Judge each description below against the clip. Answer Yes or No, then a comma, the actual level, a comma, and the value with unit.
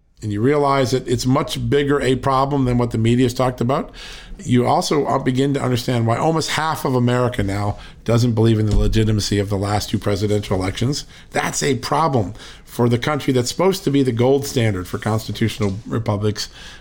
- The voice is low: Yes, low, 125 Hz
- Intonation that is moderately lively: Yes, average, 4.3 semitones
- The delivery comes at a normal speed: Yes, average, 195 wpm